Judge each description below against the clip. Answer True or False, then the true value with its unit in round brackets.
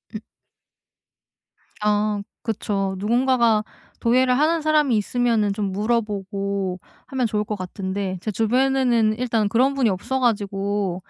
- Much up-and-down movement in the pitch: False (3.7 semitones)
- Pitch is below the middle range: False (215 Hz)